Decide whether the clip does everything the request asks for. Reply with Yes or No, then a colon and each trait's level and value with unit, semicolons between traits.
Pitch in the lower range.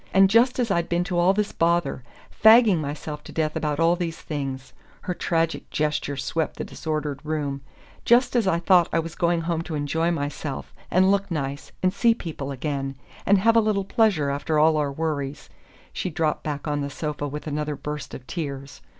No: medium, 160 Hz